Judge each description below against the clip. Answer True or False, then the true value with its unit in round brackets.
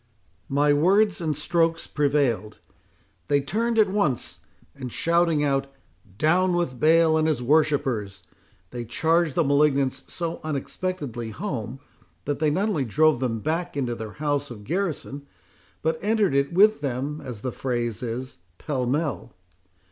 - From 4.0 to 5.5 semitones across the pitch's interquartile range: True (4.4 semitones)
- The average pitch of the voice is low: False (145 Hz)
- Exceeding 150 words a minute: False (145 wpm)